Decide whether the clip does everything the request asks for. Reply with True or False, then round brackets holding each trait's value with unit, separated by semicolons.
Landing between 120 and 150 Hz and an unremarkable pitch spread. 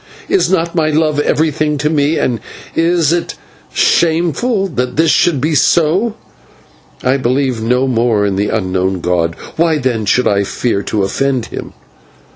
False (140 Hz; 6.3 semitones)